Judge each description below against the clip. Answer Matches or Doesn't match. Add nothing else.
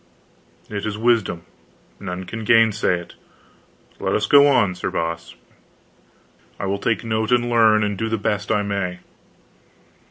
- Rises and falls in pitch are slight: Doesn't match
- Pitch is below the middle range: Matches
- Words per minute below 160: Matches